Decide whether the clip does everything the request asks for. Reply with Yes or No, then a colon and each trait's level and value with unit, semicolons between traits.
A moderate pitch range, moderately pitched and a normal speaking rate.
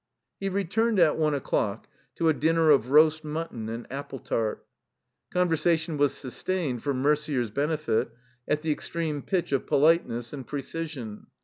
Yes: average, 3.5 semitones; medium, 150 Hz; average, 150 wpm